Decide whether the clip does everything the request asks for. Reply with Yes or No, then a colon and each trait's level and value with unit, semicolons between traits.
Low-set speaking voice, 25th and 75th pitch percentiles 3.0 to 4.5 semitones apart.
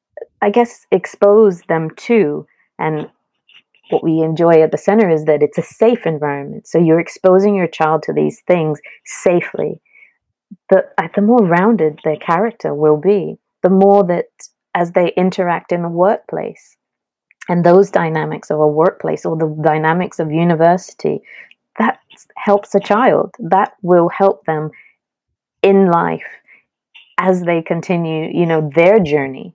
No: medium, 175 Hz; average, 3.9 semitones